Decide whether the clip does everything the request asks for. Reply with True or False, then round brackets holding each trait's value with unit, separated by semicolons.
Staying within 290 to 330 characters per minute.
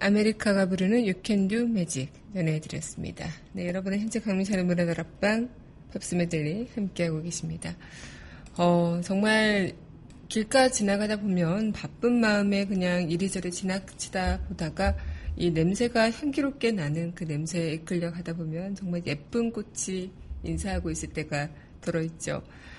True (315 characters per minute)